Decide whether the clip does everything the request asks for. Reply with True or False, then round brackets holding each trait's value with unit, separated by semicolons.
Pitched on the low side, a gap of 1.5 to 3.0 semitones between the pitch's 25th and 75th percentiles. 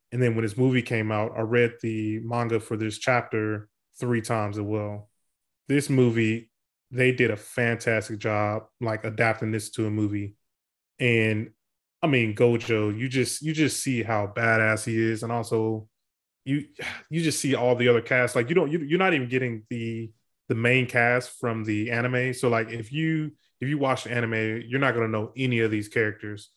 True (115 Hz; 2.4 semitones)